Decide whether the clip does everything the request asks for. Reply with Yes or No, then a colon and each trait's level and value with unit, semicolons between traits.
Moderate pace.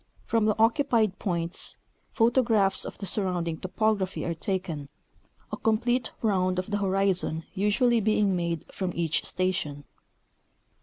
No: slow, 125 wpm